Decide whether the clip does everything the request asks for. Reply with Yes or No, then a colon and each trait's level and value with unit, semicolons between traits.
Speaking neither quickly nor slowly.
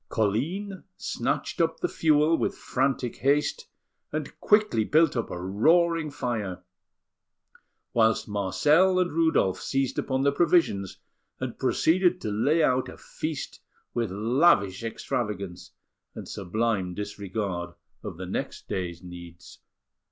No: slow, 120 wpm